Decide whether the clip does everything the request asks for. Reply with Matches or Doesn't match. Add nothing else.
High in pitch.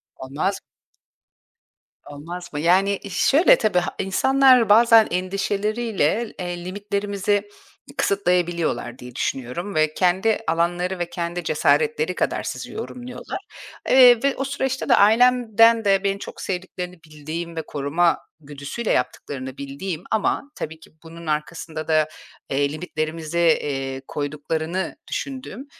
Doesn't match